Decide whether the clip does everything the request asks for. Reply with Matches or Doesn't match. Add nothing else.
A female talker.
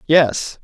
Doesn't match